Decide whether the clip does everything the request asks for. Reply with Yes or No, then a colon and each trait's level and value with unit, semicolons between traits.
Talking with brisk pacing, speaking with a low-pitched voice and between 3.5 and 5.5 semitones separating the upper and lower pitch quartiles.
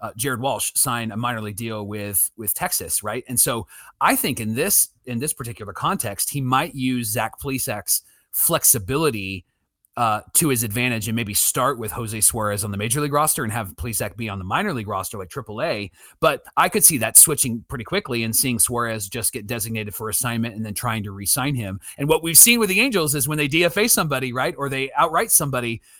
Yes: fast, 215 wpm; low, 120 Hz; average, 3.9 semitones